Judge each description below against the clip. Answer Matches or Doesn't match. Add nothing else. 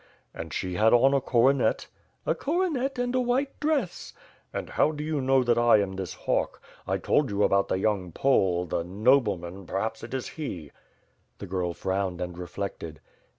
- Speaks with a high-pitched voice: Doesn't match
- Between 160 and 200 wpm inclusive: Matches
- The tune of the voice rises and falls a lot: Matches